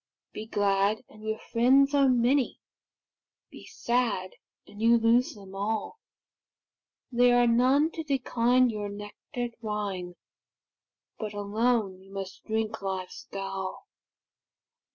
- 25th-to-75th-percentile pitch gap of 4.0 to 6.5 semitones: No, average, 3.5 semitones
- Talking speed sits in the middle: No, slow, 115 wpm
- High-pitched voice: Yes, high, 220 Hz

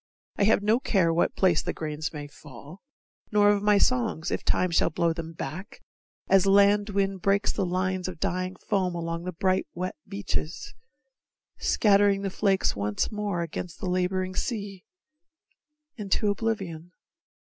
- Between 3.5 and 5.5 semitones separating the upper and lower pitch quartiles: No, average, 2.9 semitones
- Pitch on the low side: No, medium, 185 Hz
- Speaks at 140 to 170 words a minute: Yes, average, 155 wpm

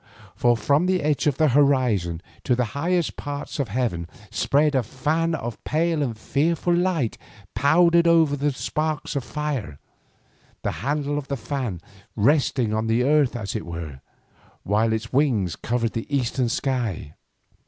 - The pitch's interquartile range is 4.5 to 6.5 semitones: Yes, average, 5.0 semitones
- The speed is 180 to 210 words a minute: No, average, 155 wpm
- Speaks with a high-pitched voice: No, low, 135 Hz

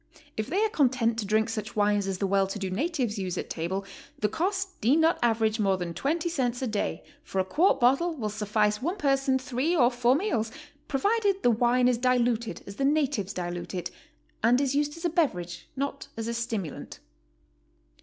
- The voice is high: Yes, high, 240 Hz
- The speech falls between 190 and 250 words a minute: Yes, average, 200 wpm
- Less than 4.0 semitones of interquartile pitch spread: No, wide, 5.5 semitones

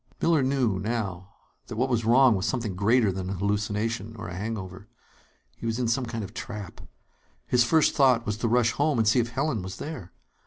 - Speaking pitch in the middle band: No, low, 115 Hz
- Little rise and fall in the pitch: No, average, 3.4 semitones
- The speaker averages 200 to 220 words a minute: Yes, fast, 205 wpm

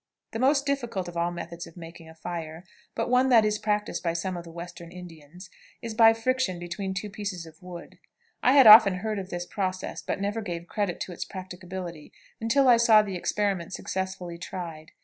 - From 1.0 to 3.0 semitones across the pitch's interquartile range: No, average, 3.8 semitones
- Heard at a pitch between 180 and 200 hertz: Yes, medium, 185 Hz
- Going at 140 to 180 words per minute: No, average, 200 wpm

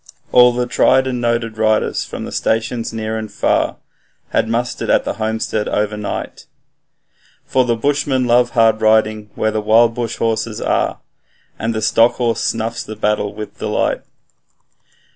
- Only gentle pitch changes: Yes, narrow, 1.7 semitones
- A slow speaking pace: No, average, 155 wpm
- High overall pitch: No, low, 115 Hz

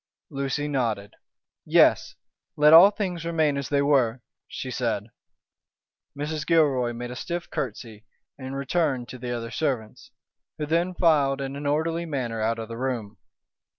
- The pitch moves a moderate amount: Yes, average, 4.4 semitones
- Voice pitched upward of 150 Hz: No, low, 135 Hz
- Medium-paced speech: Yes, average, 150 wpm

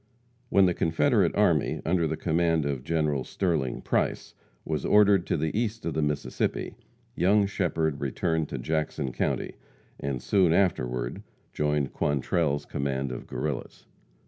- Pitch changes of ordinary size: Yes, average, 3.9 semitones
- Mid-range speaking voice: No, very low, 80 Hz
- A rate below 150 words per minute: Yes, average, 140 wpm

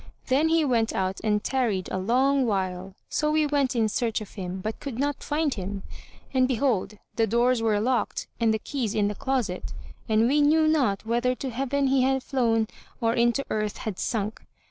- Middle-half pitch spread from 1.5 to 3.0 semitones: No, average, 4.1 semitones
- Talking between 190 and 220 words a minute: Yes, average, 195 wpm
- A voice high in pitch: Yes, high, 235 Hz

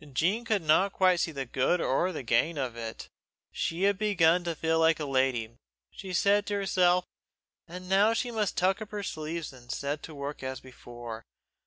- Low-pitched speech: No, medium, 165 Hz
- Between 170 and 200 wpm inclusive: Yes, average, 195 wpm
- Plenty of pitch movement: Yes, wide, 6.2 semitones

